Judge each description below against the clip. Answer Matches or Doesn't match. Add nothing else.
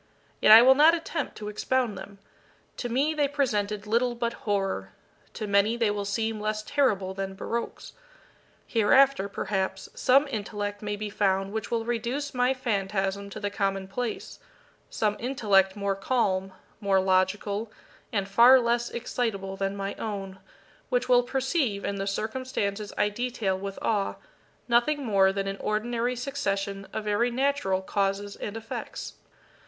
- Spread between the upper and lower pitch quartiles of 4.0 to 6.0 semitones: Doesn't match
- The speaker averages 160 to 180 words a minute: Doesn't match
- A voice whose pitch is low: Doesn't match